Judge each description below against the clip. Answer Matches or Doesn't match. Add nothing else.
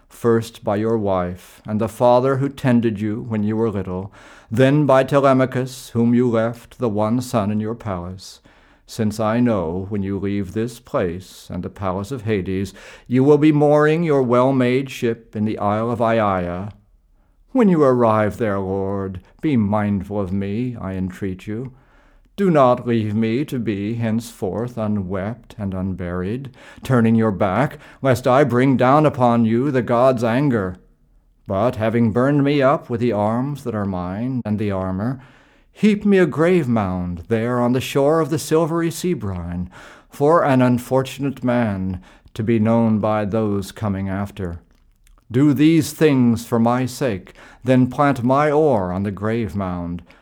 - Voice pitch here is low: Matches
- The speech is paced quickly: Doesn't match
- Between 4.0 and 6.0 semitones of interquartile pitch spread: Matches